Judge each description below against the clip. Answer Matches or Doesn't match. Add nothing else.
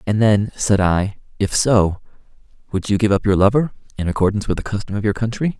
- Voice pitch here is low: Matches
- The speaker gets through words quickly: Matches